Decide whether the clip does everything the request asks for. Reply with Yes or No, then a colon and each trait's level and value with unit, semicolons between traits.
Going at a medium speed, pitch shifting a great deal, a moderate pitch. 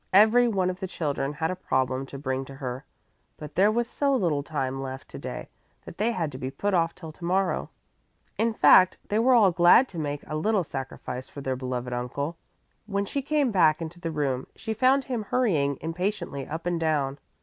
No: fast, 210 wpm; wide, 6.8 semitones; medium, 165 Hz